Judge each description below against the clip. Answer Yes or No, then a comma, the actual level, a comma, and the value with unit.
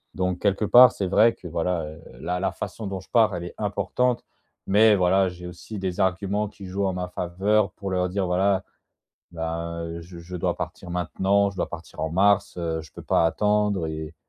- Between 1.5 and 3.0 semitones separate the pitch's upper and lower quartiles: Yes, narrow, 2.6 semitones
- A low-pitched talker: Yes, very low, 95 Hz